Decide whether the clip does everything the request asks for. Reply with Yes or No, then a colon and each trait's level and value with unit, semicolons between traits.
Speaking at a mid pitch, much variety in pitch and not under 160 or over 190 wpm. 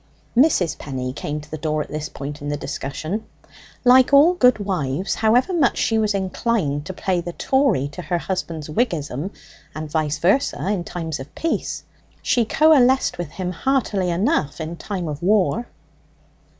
Yes: medium, 180 Hz; wide, 7.3 semitones; average, 165 wpm